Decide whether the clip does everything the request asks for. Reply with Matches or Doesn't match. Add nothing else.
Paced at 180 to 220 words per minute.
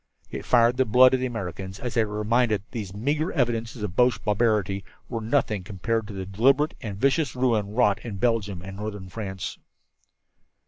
Matches